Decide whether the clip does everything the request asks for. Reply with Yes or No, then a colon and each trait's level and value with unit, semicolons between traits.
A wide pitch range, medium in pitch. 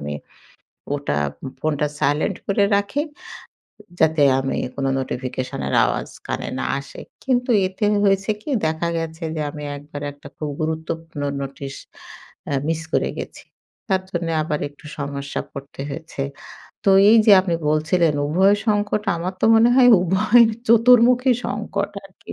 Yes: wide, 5.8 semitones; medium, 165 Hz